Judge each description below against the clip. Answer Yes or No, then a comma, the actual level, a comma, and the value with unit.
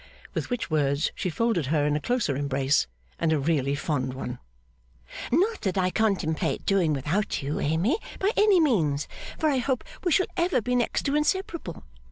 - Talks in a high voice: No, medium, 180 Hz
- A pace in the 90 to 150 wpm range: No, average, 180 wpm